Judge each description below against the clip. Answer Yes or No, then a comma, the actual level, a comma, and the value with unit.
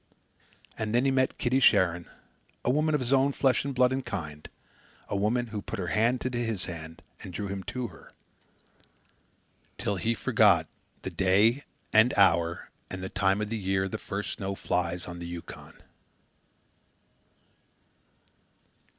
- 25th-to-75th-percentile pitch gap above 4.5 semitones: Yes, average, 4.9 semitones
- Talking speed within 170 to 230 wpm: No, average, 160 wpm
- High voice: No, low, 105 Hz